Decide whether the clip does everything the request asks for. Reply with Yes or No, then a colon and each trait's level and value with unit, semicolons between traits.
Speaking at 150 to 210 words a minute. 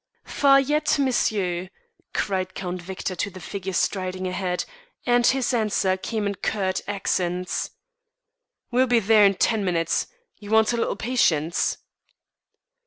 No: slow, 135 wpm